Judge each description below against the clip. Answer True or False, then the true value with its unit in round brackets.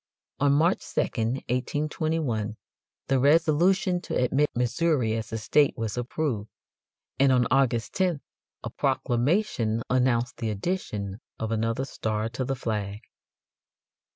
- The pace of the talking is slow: True (125 wpm)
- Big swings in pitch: False (4.9 semitones)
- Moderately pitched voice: False (125 Hz)